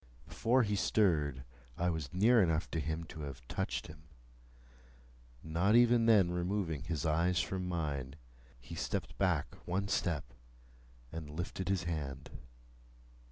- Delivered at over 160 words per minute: No, slow, 135 wpm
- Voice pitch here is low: Yes, very low, 85 Hz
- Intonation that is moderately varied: Yes, average, 4.0 semitones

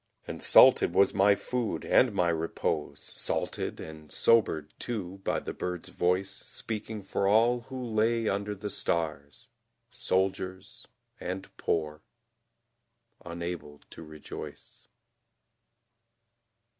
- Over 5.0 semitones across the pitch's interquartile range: No, average, 4.5 semitones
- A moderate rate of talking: No, slow, 105 wpm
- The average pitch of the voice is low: Yes, very low, 95 Hz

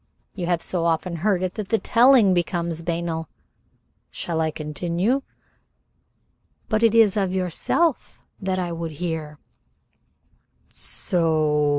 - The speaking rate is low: Yes, slow, 120 wpm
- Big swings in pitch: No, average, 3.4 semitones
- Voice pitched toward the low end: No, medium, 175 Hz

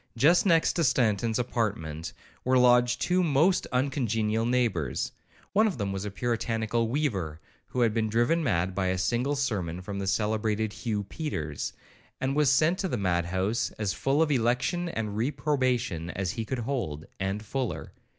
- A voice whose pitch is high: No, low, 115 Hz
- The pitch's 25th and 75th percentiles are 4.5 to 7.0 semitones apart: Yes, wide, 5.4 semitones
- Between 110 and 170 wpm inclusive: Yes, average, 165 wpm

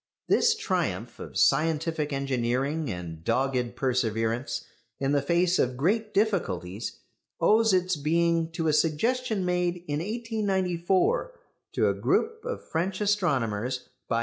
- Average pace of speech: No, slow, 130 wpm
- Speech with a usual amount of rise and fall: No, wide, 6.9 semitones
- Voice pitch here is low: No, medium, 165 Hz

